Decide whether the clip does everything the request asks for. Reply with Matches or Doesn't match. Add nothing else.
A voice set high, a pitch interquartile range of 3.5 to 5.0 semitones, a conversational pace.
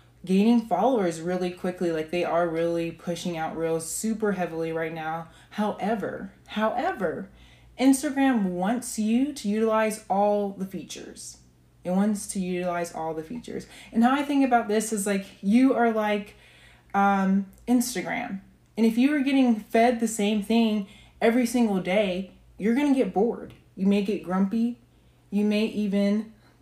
Matches